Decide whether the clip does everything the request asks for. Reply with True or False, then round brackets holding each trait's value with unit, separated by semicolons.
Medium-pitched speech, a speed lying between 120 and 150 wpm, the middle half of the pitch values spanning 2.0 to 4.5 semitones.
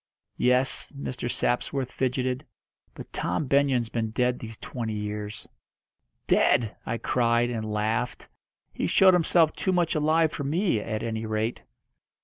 False (125 Hz; 135 wpm; 4.0 semitones)